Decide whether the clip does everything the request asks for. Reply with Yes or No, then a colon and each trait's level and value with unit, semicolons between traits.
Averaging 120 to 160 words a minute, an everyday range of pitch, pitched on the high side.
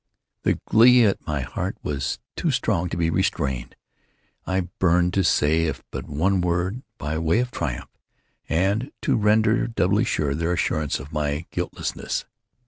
No: average, 155 wpm; average, 4.5 semitones; very low, 85 Hz